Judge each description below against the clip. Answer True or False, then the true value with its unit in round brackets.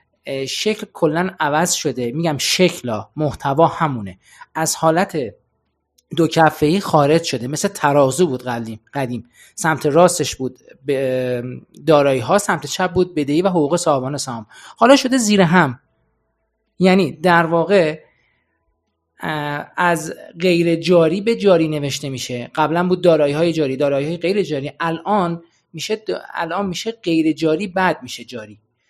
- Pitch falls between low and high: True (155 Hz)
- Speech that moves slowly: False (135 wpm)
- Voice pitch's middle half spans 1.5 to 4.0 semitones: False (5.0 semitones)